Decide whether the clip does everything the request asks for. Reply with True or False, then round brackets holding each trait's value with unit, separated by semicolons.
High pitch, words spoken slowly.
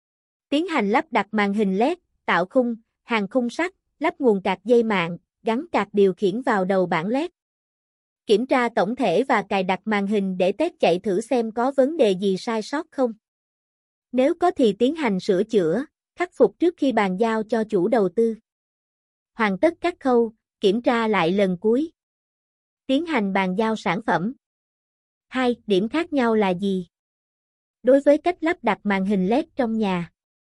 False (230 Hz; 185 wpm)